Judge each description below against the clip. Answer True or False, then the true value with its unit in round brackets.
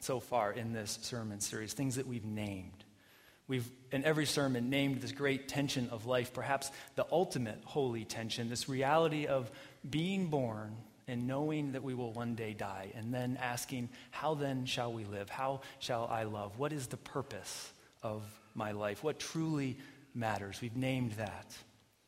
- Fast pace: False (170 wpm)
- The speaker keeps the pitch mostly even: False (3.6 semitones)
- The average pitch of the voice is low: True (125 Hz)